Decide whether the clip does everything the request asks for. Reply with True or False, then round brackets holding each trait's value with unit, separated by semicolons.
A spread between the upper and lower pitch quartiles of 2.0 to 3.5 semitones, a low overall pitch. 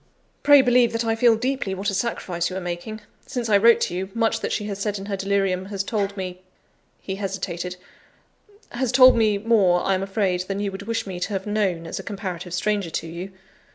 False (3.2 semitones; 200 Hz)